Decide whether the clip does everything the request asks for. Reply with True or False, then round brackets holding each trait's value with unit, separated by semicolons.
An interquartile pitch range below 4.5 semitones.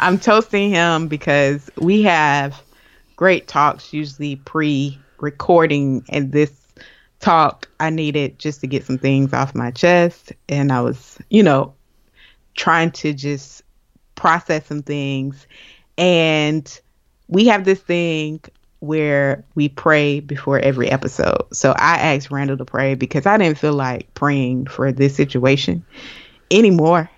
True (3.1 semitones)